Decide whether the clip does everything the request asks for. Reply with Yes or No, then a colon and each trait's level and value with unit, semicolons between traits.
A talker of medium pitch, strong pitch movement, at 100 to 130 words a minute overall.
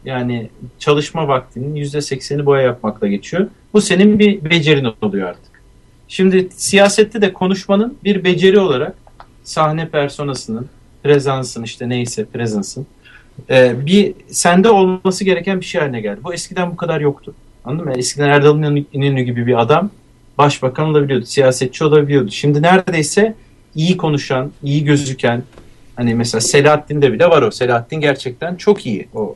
No: medium, 145 Hz; wide, 5.7 semitones; fast, 140 wpm